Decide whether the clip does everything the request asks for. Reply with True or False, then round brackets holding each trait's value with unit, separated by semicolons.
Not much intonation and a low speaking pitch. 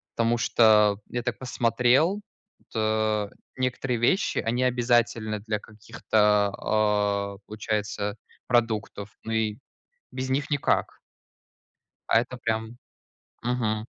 True (2.3 semitones; 115 Hz)